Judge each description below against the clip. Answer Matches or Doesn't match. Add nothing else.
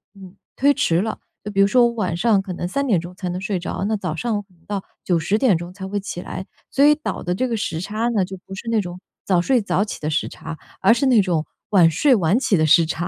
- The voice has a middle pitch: Doesn't match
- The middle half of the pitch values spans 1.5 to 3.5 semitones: Doesn't match